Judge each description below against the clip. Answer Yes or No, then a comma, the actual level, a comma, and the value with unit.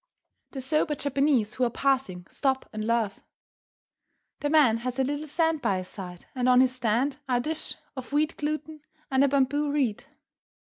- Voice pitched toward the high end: Yes, very high, 265 Hz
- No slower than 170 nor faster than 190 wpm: Yes, average, 180 wpm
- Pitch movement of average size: Yes, average, 3.7 semitones